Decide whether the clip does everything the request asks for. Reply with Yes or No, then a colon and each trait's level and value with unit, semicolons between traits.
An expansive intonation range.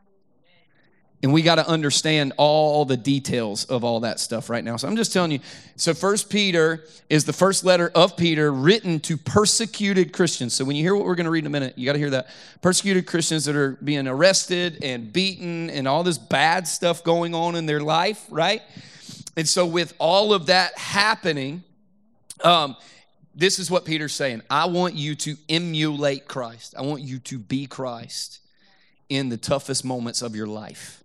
No: average, 4.5 semitones